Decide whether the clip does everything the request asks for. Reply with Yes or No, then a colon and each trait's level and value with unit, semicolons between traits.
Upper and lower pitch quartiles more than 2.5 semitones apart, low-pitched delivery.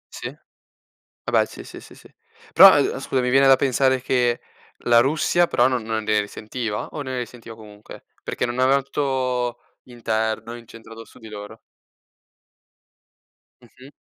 Yes: average, 2.9 semitones; low, 120 Hz